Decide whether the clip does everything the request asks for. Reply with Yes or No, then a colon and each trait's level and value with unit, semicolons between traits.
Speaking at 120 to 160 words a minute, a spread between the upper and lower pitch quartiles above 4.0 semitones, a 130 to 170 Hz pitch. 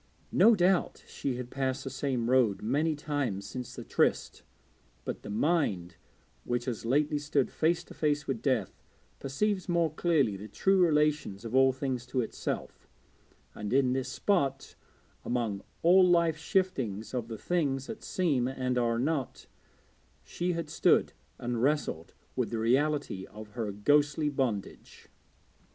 Yes: average, 150 wpm; average, 4.5 semitones; low, 135 Hz